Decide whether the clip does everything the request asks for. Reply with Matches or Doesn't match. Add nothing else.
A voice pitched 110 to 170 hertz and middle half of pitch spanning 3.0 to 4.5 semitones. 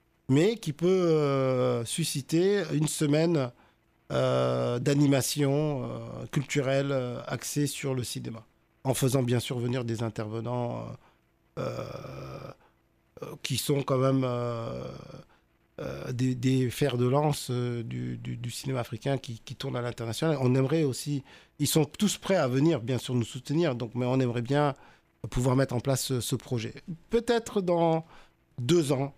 Matches